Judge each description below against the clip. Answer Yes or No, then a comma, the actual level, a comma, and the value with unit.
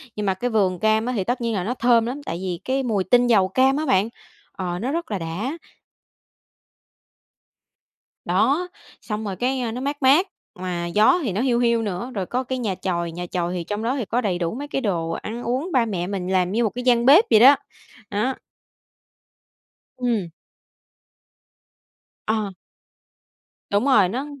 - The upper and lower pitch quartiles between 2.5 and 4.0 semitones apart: No, average, 5.1 semitones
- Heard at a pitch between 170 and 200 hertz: No, high, 220 Hz